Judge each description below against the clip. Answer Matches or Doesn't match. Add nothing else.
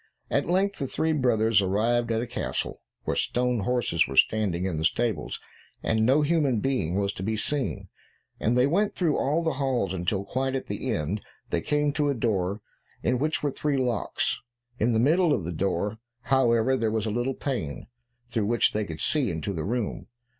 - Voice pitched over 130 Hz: Doesn't match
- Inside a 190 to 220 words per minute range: Matches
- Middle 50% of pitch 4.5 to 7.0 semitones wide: Matches